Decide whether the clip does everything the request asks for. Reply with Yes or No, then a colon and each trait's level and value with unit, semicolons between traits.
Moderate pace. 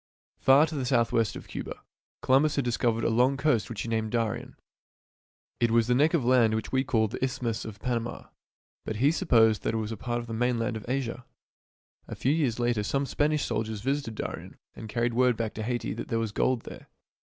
No: fast, 220 wpm